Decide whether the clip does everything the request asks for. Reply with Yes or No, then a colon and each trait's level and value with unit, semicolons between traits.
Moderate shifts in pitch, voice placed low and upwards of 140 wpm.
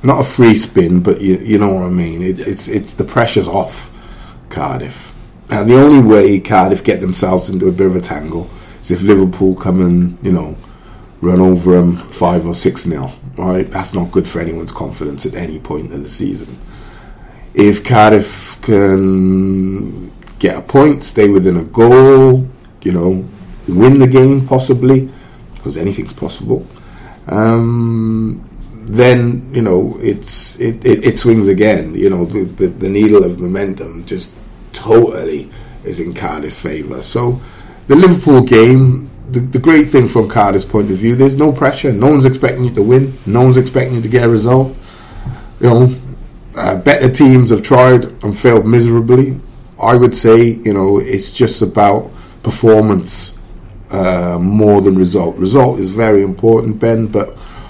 Yes: average, 5.0 semitones; low, 110 Hz; average, 165 wpm